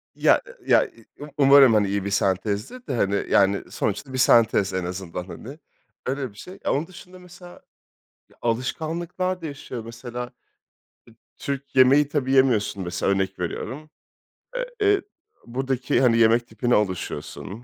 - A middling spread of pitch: No, wide, 5.9 semitones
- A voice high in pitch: No, low, 125 Hz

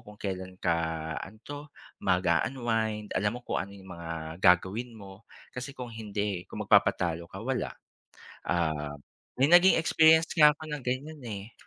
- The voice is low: Yes, low, 105 Hz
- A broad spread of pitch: Yes, wide, 5.9 semitones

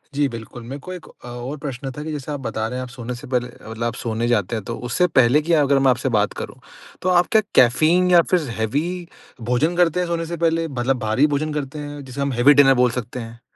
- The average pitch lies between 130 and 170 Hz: Yes, low, 135 Hz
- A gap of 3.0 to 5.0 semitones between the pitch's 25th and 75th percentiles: Yes, average, 4.2 semitones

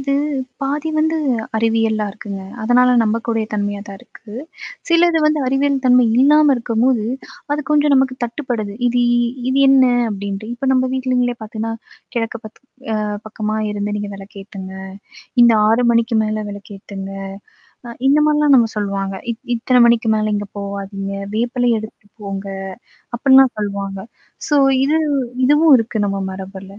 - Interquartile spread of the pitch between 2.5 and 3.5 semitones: No, average, 4.3 semitones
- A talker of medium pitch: No, high, 225 Hz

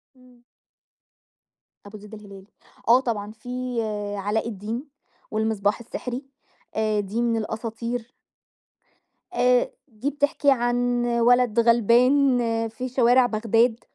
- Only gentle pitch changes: Yes, narrow, 2.3 semitones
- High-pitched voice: Yes, high, 235 Hz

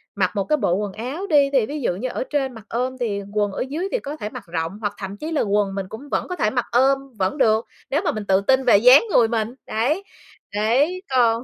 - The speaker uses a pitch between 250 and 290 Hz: No, high, 235 Hz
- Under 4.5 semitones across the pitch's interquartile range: No, average, 5.1 semitones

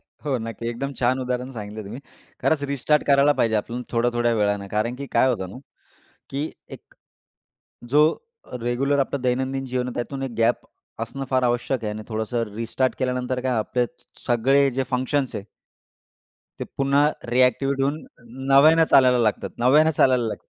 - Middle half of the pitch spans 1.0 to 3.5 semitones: Yes, narrow, 2.6 semitones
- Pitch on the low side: Yes, low, 125 Hz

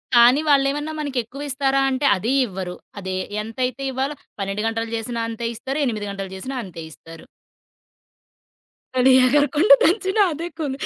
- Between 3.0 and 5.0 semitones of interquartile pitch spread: Yes, average, 4.7 semitones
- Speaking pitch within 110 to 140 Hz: No, very high, 255 Hz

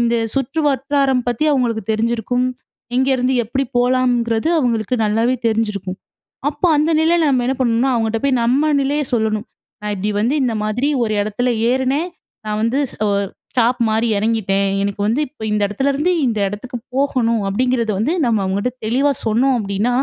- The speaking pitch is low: No, high, 240 Hz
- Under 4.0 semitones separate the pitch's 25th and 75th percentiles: Yes, average, 3.4 semitones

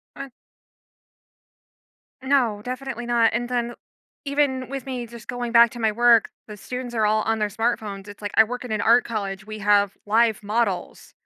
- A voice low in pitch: No, high, 235 Hz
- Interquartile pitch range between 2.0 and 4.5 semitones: Yes, narrow, 2.5 semitones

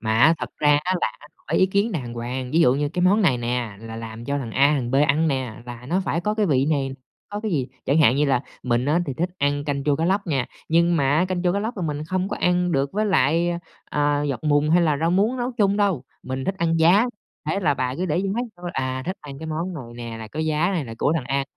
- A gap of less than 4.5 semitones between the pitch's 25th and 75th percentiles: No, average, 5.2 semitones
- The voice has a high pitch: No, medium, 150 Hz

